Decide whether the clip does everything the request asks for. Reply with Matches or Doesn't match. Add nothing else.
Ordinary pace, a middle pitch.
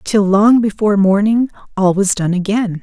Doesn't match